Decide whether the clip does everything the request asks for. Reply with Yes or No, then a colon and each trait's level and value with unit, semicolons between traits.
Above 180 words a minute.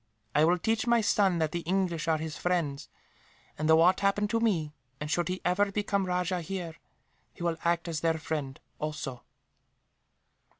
No: average, 175 wpm